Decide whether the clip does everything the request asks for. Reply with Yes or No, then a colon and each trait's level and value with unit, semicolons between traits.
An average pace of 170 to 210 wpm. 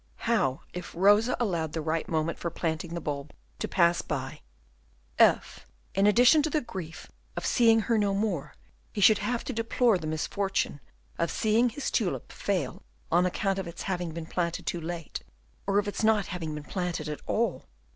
Yes: average, 185 wpm